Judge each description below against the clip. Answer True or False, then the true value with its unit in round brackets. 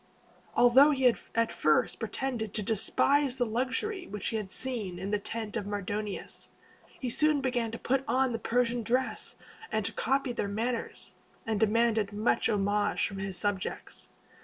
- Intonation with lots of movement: False (3.6 semitones)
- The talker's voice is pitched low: False (230 Hz)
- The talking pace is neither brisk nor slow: True (165 wpm)